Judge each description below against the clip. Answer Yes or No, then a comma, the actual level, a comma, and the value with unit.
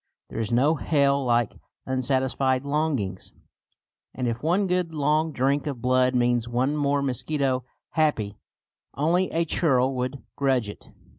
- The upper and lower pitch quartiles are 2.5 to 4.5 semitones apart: Yes, average, 3.2 semitones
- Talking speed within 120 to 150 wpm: Yes, average, 140 wpm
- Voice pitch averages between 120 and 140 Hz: Yes, low, 135 Hz